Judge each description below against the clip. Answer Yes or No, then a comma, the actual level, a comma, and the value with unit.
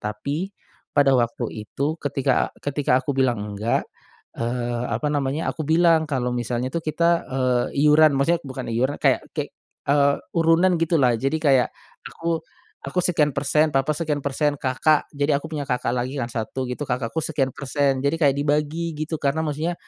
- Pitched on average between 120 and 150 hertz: Yes, medium, 140 Hz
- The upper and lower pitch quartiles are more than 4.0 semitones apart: No, average, 3.3 semitones